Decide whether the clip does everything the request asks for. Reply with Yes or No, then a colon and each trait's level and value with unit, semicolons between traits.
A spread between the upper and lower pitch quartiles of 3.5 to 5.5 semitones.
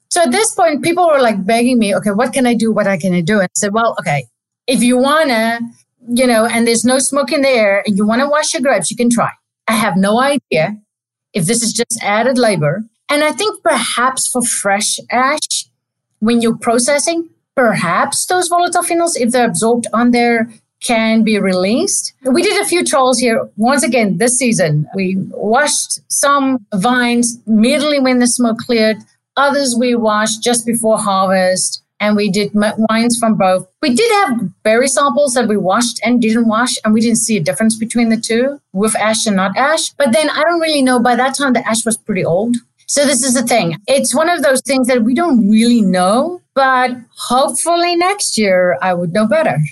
Yes: average, 4.2 semitones